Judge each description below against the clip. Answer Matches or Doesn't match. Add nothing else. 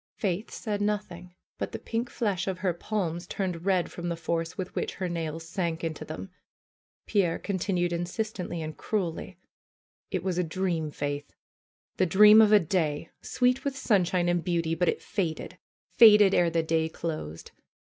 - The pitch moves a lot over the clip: Doesn't match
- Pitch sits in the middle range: Matches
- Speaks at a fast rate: Doesn't match